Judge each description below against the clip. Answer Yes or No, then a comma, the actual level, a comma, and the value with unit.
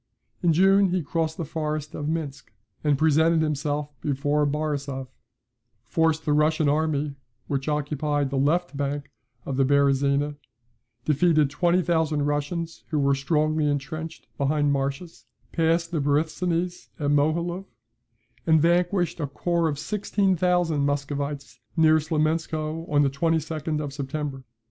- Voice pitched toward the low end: No, medium, 150 Hz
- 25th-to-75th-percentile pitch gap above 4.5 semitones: No, narrow, 2.4 semitones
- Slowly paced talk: Yes, slow, 130 wpm